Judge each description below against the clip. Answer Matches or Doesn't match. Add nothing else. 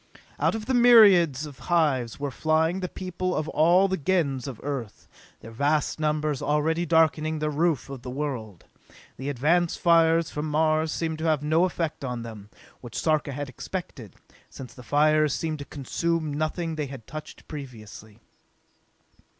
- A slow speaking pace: Doesn't match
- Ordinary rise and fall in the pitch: Matches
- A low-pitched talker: Doesn't match